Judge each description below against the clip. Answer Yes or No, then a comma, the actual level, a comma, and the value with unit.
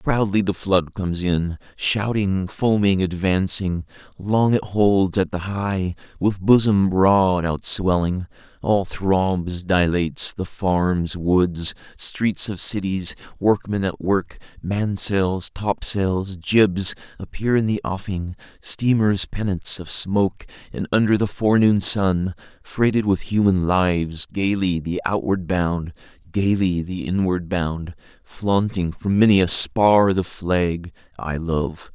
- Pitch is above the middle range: No, very low, 95 Hz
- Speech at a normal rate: No, slow, 120 wpm